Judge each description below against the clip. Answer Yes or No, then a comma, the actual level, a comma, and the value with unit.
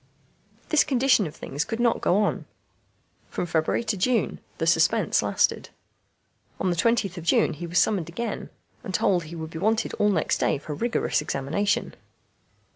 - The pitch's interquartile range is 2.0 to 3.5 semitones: No, wide, 5.6 semitones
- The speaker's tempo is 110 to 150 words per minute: No, average, 175 wpm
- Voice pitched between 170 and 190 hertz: Yes, medium, 185 Hz